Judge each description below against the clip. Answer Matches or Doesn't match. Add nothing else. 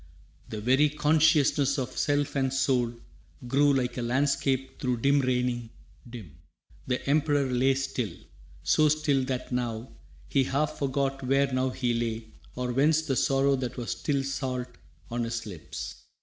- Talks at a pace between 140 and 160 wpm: Matches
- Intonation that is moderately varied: Doesn't match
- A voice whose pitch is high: Doesn't match